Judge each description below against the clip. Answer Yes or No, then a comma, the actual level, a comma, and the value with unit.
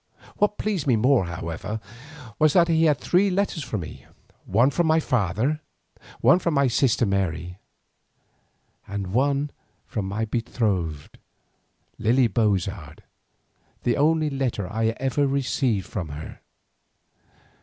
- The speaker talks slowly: Yes, slow, 125 wpm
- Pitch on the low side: Yes, low, 120 Hz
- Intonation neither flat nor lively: No, wide, 7.0 semitones